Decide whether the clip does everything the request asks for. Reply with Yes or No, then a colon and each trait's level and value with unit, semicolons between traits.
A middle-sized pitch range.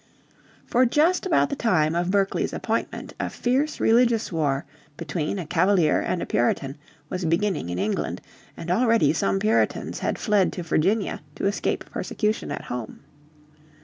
No: wide, 6.2 semitones